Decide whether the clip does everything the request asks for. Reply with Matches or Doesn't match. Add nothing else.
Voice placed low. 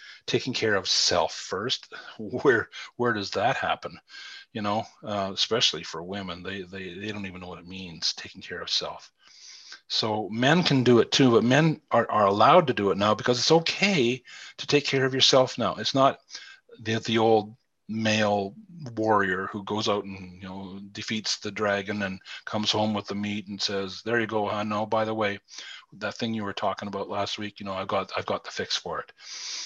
Matches